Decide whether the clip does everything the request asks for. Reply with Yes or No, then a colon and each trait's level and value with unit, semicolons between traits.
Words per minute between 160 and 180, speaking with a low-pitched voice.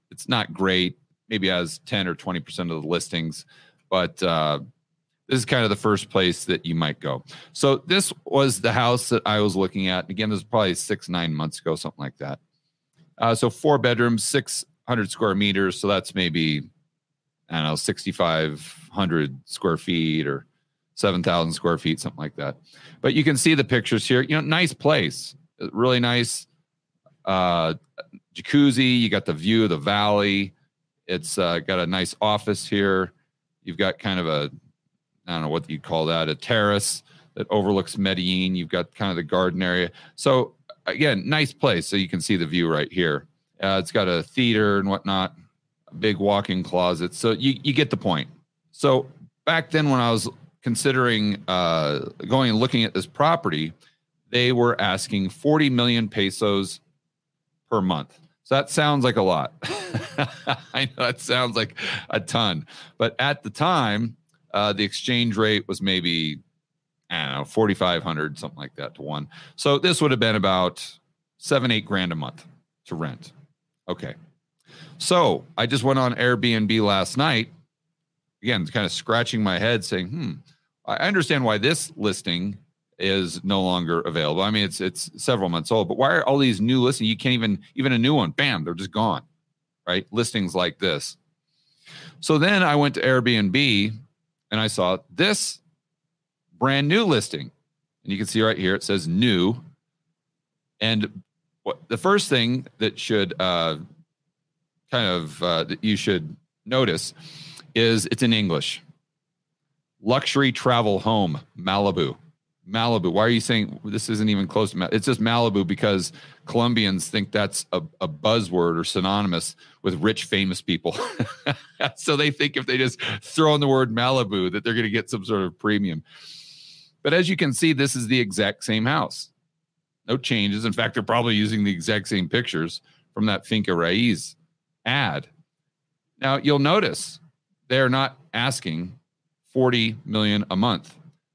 Yes: average, 170 wpm; low, 120 Hz